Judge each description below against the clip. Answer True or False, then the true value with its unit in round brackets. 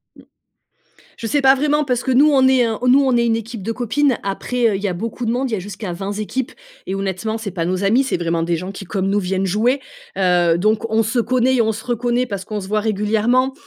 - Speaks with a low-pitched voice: False (220 Hz)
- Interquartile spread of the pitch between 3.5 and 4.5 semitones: True (4.2 semitones)